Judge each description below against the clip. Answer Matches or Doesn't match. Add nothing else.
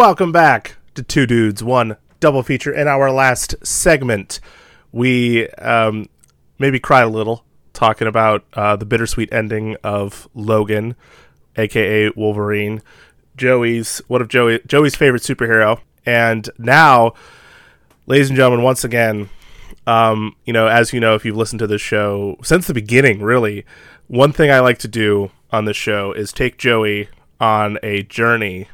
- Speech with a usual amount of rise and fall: Matches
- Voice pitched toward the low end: Matches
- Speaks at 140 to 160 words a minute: Matches